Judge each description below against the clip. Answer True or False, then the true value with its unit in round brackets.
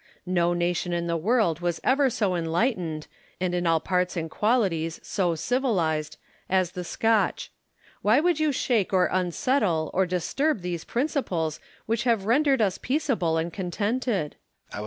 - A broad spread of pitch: True (5.7 semitones)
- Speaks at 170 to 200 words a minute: False (155 wpm)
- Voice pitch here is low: False (185 Hz)